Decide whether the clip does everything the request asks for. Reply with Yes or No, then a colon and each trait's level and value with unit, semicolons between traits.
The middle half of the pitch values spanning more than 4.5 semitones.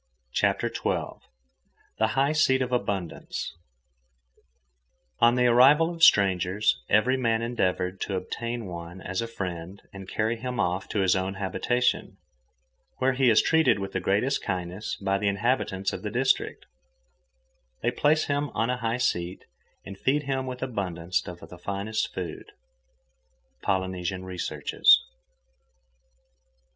Yes: average, 5.3 semitones